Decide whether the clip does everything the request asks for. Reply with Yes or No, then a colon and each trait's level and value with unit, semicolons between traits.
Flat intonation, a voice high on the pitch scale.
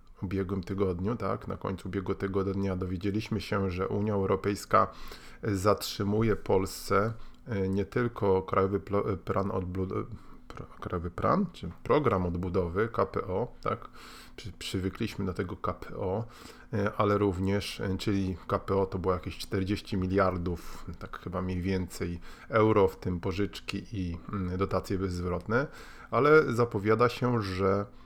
No: narrow, 1.8 semitones; very low, 95 Hz